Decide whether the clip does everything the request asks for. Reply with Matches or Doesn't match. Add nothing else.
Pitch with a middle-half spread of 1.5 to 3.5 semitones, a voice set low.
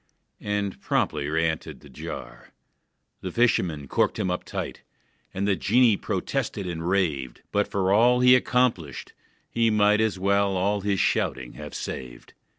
Doesn't match